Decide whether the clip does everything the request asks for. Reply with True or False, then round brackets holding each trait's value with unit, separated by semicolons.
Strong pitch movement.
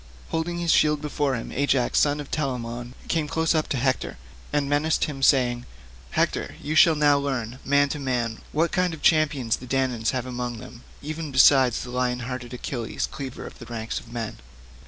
False (3.4 semitones)